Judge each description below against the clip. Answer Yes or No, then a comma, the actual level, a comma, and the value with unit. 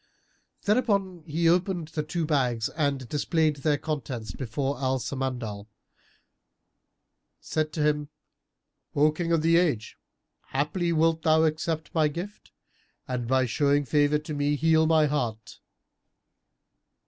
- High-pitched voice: No, medium, 150 Hz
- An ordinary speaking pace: No, slow, 125 wpm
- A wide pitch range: No, average, 3.3 semitones